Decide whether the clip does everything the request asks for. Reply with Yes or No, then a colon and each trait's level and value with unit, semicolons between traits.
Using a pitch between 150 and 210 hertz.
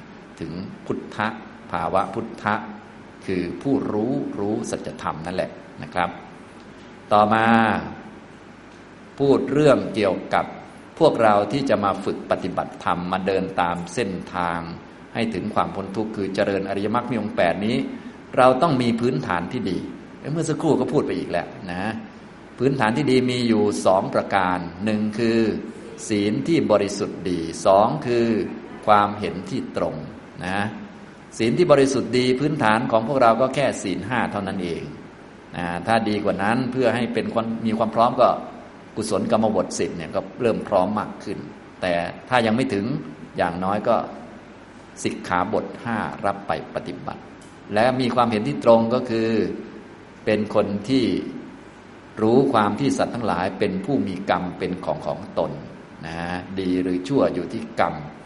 No: low, 110 Hz